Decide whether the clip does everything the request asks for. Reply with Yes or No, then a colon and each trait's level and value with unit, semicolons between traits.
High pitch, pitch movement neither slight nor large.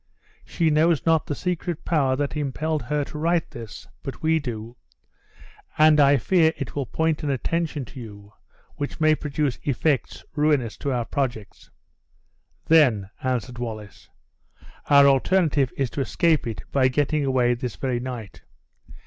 No: medium, 140 Hz; average, 4.1 semitones